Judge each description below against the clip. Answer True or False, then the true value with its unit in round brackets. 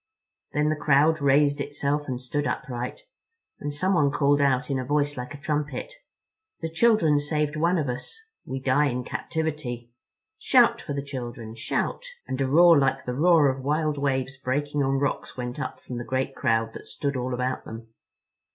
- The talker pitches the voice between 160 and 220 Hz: False (140 Hz)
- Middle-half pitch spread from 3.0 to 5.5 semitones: False (2.6 semitones)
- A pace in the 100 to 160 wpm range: False (180 wpm)